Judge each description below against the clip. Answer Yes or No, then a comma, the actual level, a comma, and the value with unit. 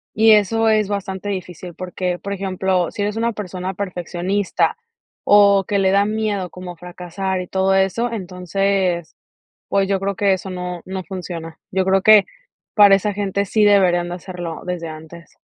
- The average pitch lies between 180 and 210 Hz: Yes, high, 190 Hz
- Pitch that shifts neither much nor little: No, narrow, 2.0 semitones